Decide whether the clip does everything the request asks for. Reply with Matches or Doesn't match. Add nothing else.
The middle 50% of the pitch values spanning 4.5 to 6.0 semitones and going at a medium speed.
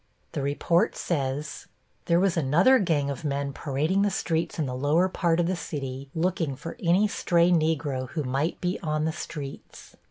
Doesn't match